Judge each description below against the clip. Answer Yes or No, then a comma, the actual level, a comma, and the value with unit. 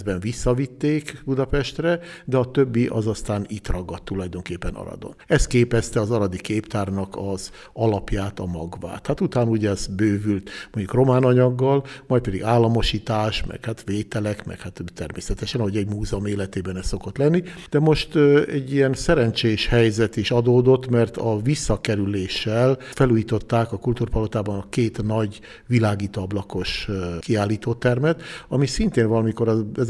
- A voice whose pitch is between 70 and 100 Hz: No, low, 110 Hz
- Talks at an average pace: Yes, average, 135 wpm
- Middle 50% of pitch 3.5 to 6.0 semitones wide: Yes, average, 4.0 semitones